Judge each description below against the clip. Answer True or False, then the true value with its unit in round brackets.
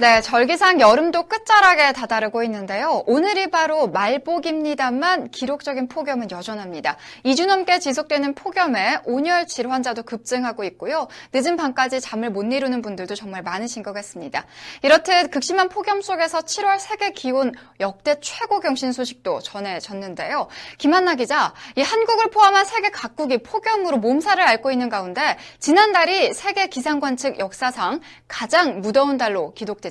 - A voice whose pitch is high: True (275 Hz)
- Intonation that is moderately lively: False (7.3 semitones)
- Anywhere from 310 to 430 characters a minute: True (355 characters per minute)